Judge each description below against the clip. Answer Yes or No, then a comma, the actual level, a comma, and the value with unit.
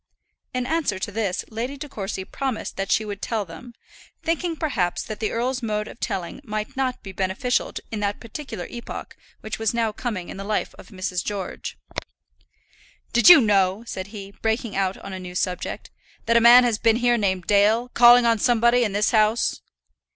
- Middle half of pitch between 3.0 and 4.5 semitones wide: Yes, average, 3.5 semitones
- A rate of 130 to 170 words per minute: No, average, 190 wpm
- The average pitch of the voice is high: Yes, high, 220 Hz